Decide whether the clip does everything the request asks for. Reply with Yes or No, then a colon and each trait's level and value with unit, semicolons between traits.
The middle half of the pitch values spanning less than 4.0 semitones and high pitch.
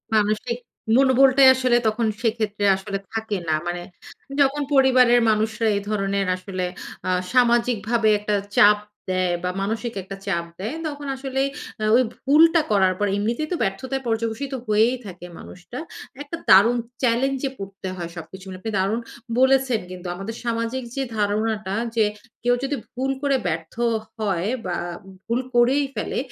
No: average, 4.6 semitones; high, 225 Hz